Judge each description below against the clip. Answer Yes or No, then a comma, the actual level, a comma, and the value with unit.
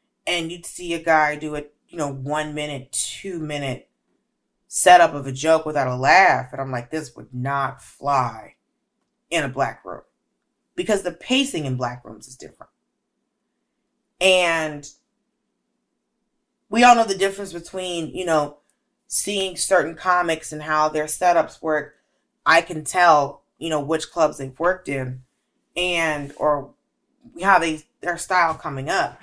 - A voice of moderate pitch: Yes, medium, 160 Hz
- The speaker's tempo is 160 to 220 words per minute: No, average, 150 wpm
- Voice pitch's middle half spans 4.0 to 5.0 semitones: No, average, 3.5 semitones